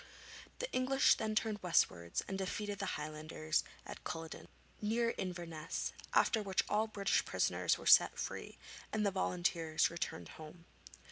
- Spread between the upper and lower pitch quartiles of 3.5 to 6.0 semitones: Yes, average, 4.8 semitones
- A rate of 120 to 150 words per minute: Yes, average, 140 wpm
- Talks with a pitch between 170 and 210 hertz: Yes, medium, 185 Hz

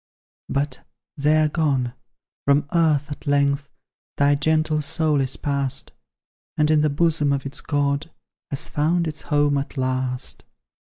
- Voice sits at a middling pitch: Yes, medium, 145 Hz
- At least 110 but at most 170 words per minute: Yes, average, 145 wpm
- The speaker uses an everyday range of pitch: No, narrow, 1.6 semitones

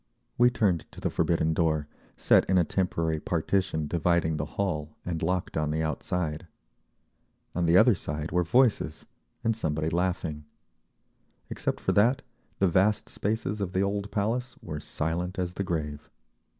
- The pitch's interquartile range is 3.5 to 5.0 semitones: Yes, average, 3.9 semitones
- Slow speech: No, average, 155 wpm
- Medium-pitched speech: No, very low, 85 Hz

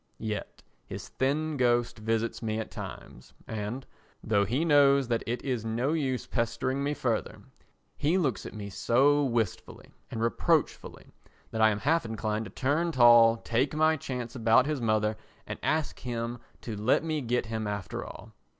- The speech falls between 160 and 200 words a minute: Yes, average, 170 wpm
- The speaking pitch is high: No, low, 120 Hz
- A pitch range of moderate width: Yes, average, 3.8 semitones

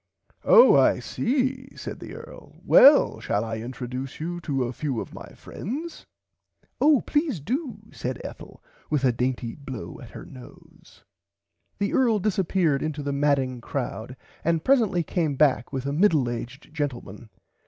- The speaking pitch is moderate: Yes, medium, 145 Hz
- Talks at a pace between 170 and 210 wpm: No, average, 155 wpm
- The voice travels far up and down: Yes, wide, 8.3 semitones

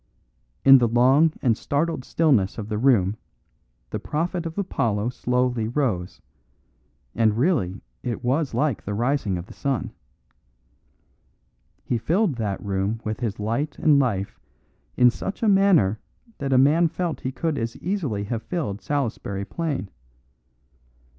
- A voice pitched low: Yes, low, 125 Hz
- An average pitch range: No, wide, 6.0 semitones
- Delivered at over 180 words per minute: No, average, 140 wpm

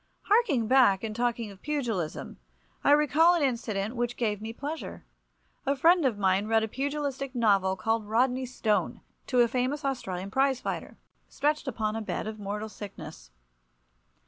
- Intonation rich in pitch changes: No, average, 4.5 semitones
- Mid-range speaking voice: No, high, 235 Hz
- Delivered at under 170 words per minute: Yes, average, 160 wpm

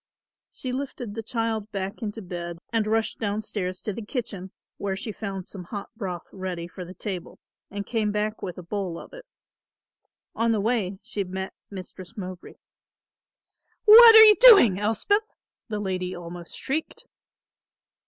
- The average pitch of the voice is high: Yes, high, 205 Hz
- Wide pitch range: No, average, 3.5 semitones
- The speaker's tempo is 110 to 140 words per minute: No, average, 160 wpm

